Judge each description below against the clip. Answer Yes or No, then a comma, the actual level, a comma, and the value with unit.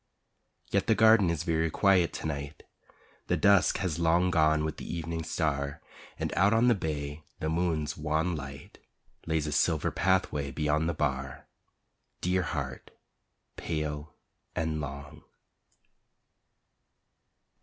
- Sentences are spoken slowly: Yes, slow, 130 wpm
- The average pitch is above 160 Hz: No, very low, 80 Hz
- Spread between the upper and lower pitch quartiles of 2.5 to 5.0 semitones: Yes, average, 2.8 semitones